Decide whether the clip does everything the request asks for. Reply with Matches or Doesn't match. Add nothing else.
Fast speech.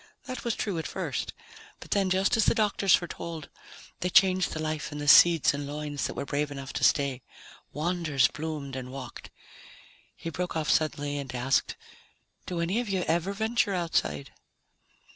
Doesn't match